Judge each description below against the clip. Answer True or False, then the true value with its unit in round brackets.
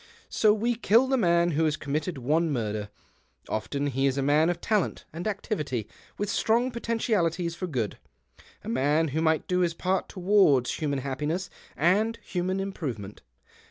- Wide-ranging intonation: True (5.7 semitones)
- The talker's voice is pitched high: False (165 Hz)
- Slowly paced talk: False (160 wpm)